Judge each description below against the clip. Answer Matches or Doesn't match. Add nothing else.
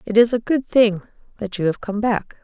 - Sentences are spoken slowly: Doesn't match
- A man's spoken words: Doesn't match